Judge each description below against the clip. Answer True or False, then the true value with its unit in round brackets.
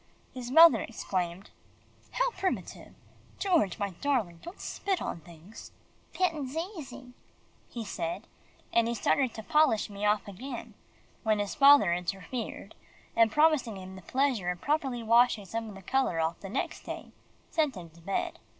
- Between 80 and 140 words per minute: False (160 wpm)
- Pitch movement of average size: False (6.4 semitones)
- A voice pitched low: False (225 Hz)